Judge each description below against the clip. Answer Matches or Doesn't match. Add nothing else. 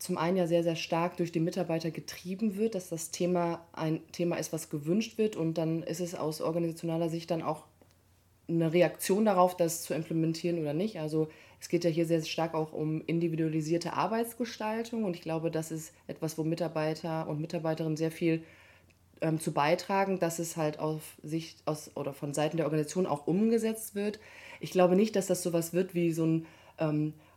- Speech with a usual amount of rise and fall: Doesn't match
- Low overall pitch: Doesn't match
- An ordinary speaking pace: Doesn't match